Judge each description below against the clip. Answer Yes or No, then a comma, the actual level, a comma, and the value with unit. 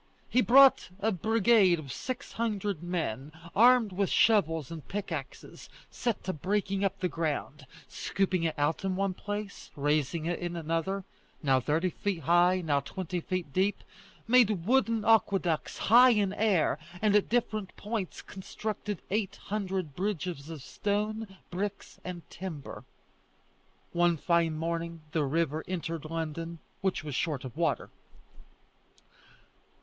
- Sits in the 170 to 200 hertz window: Yes, medium, 185 Hz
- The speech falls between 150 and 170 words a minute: No, slow, 135 wpm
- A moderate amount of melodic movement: Yes, average, 4.0 semitones